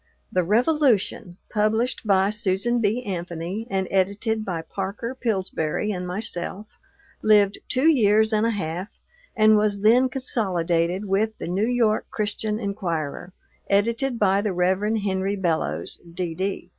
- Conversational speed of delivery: No, slow, 130 wpm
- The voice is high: Yes, high, 205 Hz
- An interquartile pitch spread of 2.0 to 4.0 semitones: Yes, average, 3.0 semitones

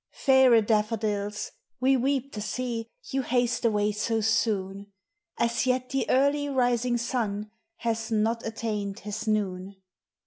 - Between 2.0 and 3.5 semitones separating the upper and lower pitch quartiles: Yes, average, 3.1 semitones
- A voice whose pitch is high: Yes, high, 225 Hz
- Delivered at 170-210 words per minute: No, average, 140 wpm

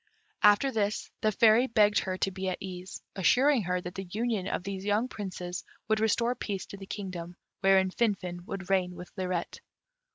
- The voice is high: Yes, high, 195 Hz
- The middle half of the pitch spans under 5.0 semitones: Yes, average, 2.7 semitones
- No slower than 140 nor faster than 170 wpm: No, average, 185 wpm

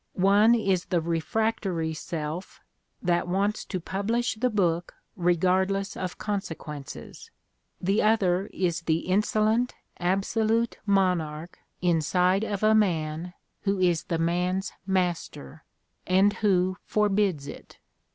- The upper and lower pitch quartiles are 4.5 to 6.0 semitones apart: No, average, 3.1 semitones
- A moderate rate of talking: No, slow, 115 wpm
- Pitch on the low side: No, medium, 185 Hz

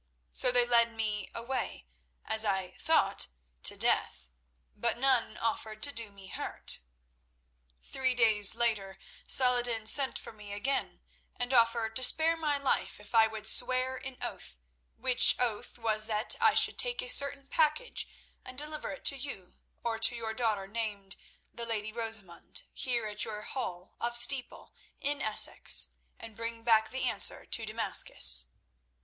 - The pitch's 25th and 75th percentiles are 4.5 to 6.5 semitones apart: No, average, 3.1 semitones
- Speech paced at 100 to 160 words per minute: Yes, average, 155 wpm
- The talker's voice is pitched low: No, high, 230 Hz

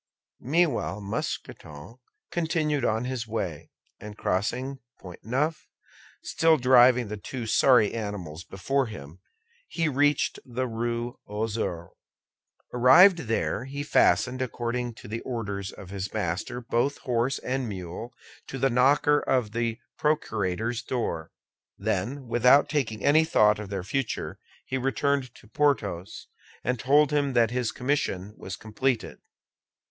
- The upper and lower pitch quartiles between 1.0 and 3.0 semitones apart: No, average, 4.3 semitones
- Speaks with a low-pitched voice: Yes, low, 120 Hz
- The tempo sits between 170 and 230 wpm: No, slow, 135 wpm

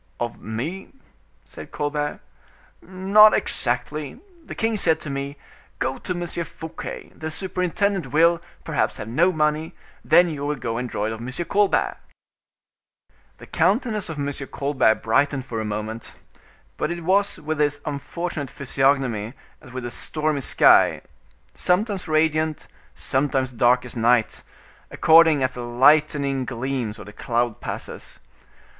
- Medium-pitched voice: Yes, medium, 145 Hz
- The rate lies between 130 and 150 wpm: Yes, average, 140 wpm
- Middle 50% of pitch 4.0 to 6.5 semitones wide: Yes, average, 5.2 semitones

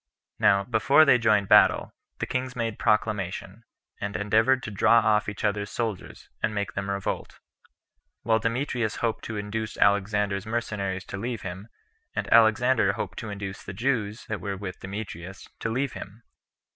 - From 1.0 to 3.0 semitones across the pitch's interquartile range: Yes, narrow, 2.6 semitones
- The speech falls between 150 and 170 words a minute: Yes, average, 160 wpm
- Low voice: Yes, low, 105 Hz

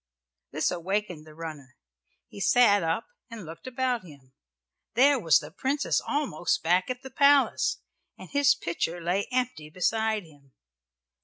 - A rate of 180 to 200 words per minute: No, average, 145 wpm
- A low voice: No, high, 195 Hz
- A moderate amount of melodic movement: No, wide, 7.6 semitones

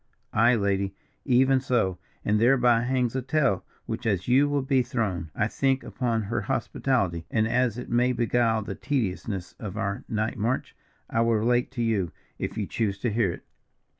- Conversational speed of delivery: Yes, average, 180 wpm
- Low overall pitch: Yes, low, 115 Hz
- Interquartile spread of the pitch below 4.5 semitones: Yes, average, 3.6 semitones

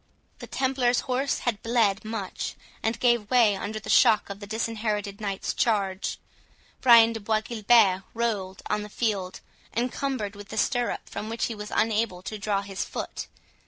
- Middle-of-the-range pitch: No, high, 215 Hz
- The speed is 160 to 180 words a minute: Yes, average, 165 wpm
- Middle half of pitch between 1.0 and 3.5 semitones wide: Yes, narrow, 2.6 semitones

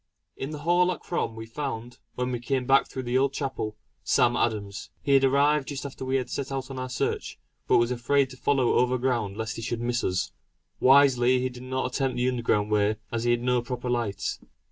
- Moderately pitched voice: No, low, 125 Hz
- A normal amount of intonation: No, narrow, 2.3 semitones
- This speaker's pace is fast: Yes, fast, 225 wpm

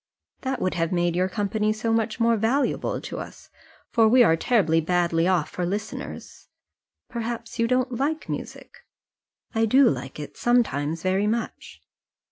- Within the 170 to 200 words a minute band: No, average, 155 wpm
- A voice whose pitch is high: Yes, high, 215 Hz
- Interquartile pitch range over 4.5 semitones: Yes, average, 5.1 semitones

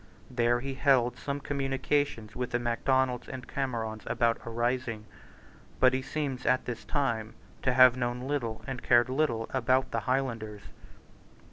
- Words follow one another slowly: No, average, 150 wpm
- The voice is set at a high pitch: No, low, 125 Hz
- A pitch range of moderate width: No, narrow, 2.2 semitones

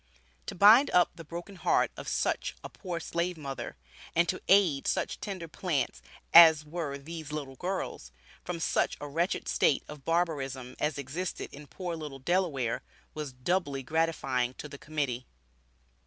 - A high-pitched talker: No, medium, 155 Hz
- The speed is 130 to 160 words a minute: Yes, average, 155 wpm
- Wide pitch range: No, average, 4.1 semitones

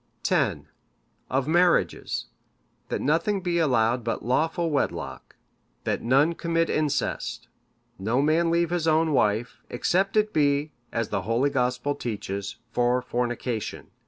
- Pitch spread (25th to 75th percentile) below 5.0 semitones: No, wide, 5.4 semitones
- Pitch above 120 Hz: Yes, medium, 140 Hz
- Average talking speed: No, slow, 130 wpm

